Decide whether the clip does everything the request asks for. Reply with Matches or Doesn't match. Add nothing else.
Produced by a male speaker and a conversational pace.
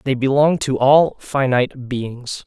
Matches